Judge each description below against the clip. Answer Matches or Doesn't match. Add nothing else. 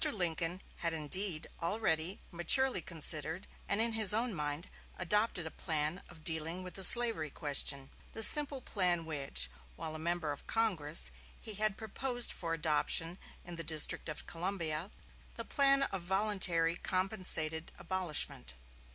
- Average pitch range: Matches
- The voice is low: Doesn't match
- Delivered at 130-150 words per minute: Matches